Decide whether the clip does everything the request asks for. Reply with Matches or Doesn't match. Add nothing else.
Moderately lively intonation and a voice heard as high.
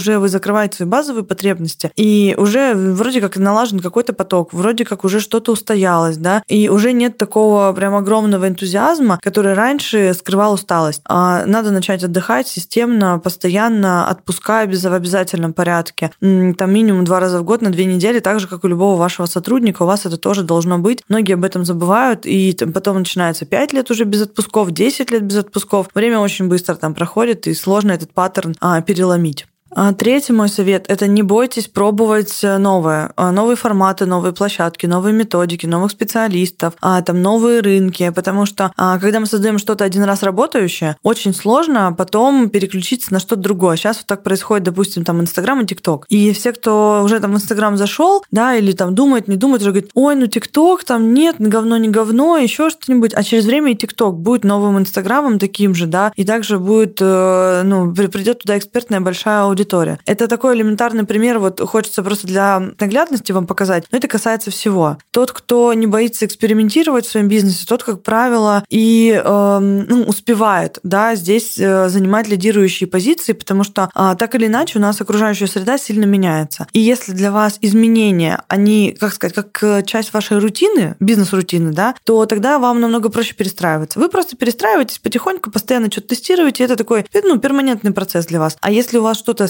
Matches